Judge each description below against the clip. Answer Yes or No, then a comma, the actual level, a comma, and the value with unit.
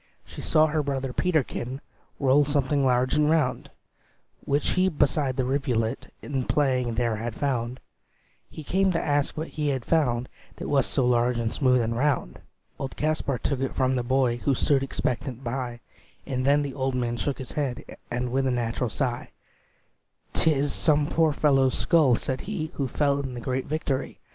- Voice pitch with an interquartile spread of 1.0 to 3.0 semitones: Yes, average, 2.7 semitones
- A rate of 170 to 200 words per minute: Yes, average, 180 wpm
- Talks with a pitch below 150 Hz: Yes, low, 135 Hz